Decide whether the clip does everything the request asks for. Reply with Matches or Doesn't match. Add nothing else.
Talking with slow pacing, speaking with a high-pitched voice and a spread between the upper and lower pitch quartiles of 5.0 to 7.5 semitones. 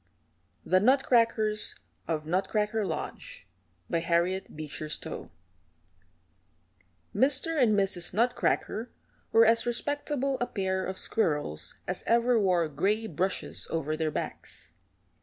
Matches